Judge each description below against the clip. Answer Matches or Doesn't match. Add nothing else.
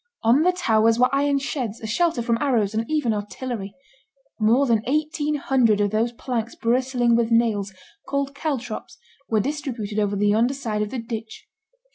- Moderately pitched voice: Doesn't match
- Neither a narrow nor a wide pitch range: Matches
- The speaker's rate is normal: Matches